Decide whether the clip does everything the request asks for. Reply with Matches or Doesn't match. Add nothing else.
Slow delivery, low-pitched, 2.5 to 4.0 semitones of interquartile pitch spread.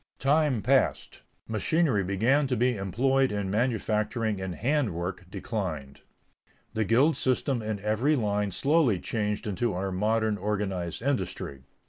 Doesn't match